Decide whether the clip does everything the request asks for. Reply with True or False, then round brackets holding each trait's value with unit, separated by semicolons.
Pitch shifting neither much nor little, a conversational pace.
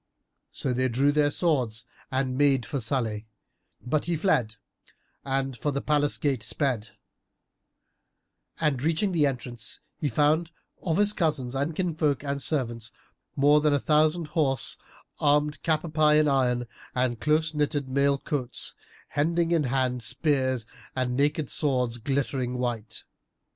True (3.2 semitones; 145 wpm)